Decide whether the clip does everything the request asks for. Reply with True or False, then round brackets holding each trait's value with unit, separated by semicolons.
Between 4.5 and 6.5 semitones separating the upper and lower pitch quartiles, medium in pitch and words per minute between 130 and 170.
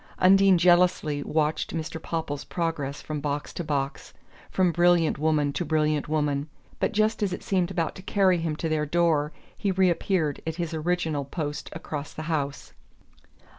False (3.0 semitones; 160 Hz; 165 wpm)